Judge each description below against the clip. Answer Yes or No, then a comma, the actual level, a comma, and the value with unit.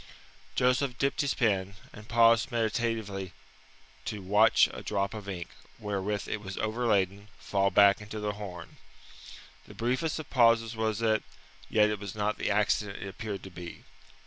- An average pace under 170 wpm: Yes, average, 160 wpm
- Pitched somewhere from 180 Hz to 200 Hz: No, low, 105 Hz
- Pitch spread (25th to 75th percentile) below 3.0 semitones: Yes, narrow, 2.5 semitones